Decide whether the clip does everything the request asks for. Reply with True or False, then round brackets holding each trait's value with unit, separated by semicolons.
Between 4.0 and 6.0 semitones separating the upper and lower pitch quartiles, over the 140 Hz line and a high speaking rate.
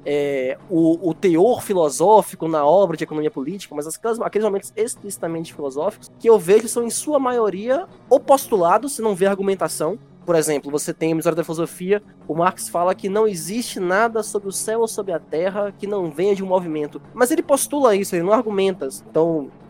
True (5.0 semitones; 190 Hz; 195 wpm)